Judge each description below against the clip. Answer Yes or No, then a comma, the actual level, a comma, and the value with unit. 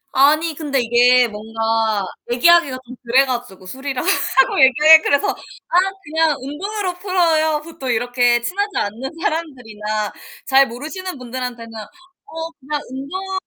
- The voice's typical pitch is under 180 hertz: No, very high, 270 Hz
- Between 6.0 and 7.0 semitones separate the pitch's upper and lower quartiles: No, average, 5.3 semitones